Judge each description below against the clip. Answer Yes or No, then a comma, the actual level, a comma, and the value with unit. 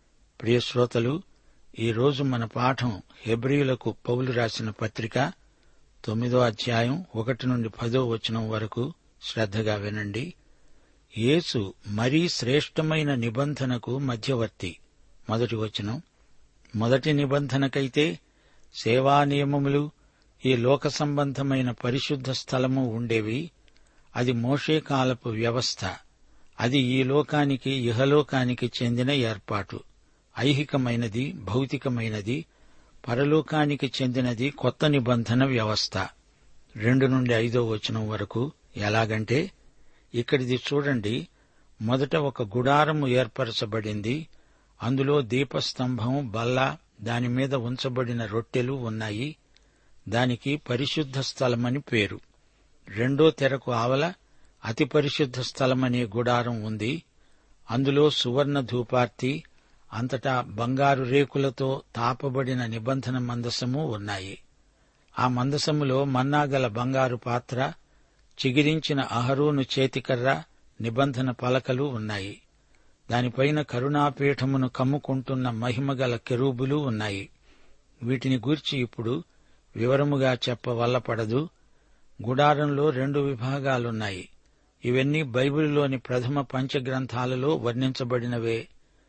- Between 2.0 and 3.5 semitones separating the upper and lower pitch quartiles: Yes, average, 2.8 semitones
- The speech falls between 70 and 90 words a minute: Yes, average, 85 wpm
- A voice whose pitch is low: Yes, low, 130 Hz